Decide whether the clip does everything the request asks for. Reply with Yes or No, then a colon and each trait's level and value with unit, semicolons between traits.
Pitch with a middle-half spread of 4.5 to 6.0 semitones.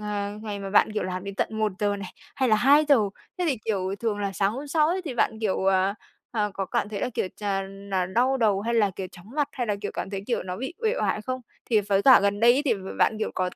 No: average, 4.0 semitones